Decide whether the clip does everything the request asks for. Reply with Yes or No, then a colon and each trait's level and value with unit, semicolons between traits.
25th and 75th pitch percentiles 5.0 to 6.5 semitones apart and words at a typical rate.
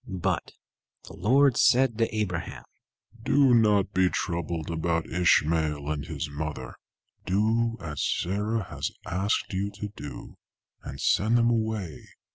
No: average, 5.3 semitones; slow, 130 wpm